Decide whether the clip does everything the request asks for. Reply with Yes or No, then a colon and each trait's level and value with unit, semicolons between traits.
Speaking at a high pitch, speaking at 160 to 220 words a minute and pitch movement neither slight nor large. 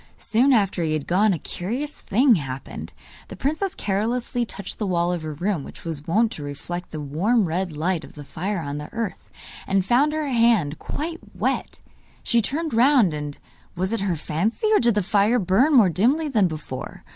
No: high, 195 Hz; average, 195 wpm; wide, 6.5 semitones